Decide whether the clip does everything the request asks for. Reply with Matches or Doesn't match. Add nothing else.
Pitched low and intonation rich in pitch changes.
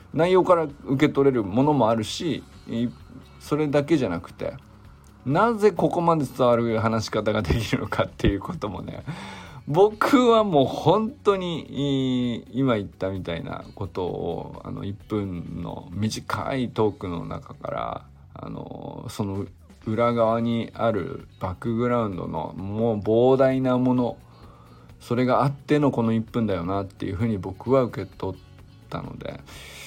Matches